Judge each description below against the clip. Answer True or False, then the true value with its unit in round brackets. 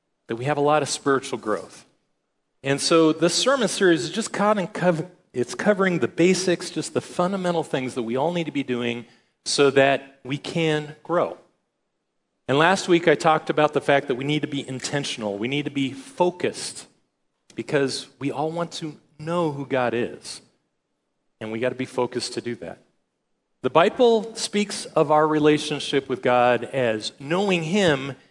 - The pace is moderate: True (175 wpm)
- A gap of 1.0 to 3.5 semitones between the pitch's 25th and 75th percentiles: False (4.5 semitones)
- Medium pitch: True (150 Hz)